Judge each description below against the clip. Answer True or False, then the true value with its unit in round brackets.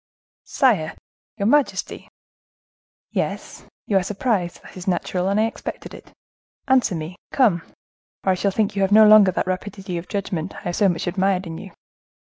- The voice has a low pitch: False (195 Hz)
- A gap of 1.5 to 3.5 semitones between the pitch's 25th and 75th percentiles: True (2.7 semitones)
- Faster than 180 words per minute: False (175 wpm)